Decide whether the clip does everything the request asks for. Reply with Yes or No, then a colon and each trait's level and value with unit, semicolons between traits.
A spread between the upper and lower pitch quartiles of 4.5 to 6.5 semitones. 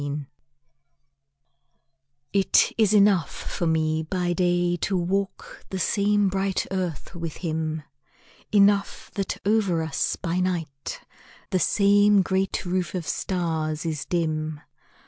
No: average, 3.5 semitones